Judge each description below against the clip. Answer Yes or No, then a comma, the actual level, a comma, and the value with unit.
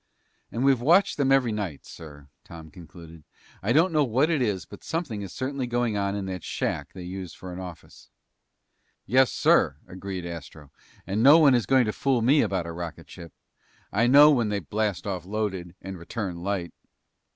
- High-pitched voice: No, low, 100 Hz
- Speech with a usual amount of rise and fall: No, wide, 6.5 semitones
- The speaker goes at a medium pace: Yes, average, 190 wpm